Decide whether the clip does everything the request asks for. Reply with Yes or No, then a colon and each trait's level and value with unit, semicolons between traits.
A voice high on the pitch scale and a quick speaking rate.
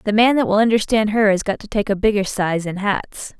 Yes: high, 210 Hz; fast, 265 wpm